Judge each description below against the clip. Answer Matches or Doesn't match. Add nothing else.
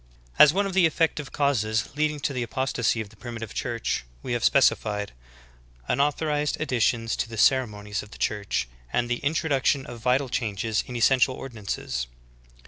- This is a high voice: Doesn't match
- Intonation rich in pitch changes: Doesn't match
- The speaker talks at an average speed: Matches